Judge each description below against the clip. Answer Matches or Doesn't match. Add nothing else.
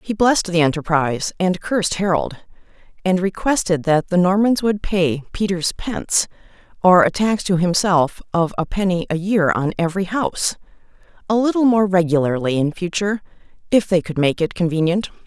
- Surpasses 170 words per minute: Doesn't match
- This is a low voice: Doesn't match